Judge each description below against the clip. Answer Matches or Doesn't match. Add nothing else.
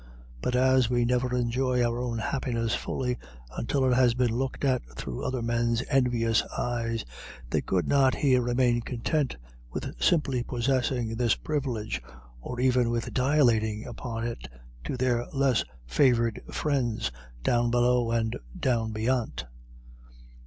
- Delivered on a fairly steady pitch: Matches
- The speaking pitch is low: Matches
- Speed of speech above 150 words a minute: Doesn't match